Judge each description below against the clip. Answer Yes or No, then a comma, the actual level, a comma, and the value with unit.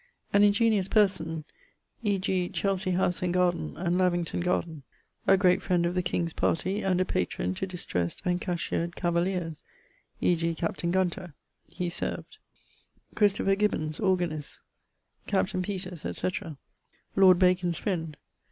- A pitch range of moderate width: No, narrow, 2.0 semitones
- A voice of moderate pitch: Yes, medium, 180 Hz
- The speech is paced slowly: Yes, slow, 130 wpm